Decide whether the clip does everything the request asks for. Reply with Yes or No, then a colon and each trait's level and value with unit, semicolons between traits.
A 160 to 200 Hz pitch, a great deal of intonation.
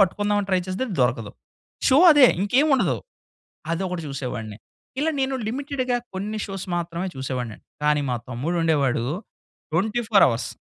Yes: medium, 185 Hz; wide, 8.5 semitones